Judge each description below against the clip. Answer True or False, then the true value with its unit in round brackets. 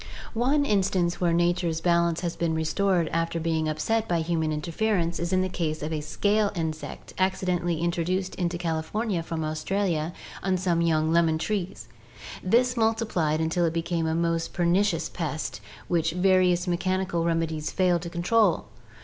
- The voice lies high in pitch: False (170 Hz)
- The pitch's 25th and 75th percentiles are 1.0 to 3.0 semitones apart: True (2.4 semitones)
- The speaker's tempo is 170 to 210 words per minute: False (160 wpm)